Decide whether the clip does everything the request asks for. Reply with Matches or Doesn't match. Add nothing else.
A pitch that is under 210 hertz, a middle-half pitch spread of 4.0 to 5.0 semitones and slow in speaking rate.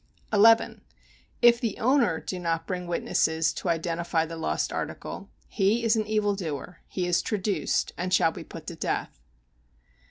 Doesn't match